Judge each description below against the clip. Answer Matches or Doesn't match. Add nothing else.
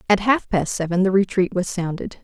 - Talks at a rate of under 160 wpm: Doesn't match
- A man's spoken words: Doesn't match